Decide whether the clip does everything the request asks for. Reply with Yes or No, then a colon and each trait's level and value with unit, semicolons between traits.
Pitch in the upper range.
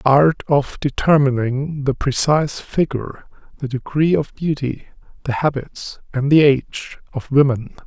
No: medium, 140 Hz